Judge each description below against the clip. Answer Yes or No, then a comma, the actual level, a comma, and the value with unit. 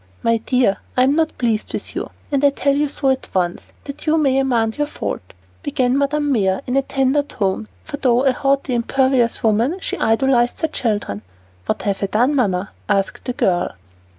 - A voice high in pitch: Yes, very high, 255 Hz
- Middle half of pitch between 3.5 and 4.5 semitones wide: Yes, average, 4.1 semitones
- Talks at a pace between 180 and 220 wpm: Yes, average, 190 wpm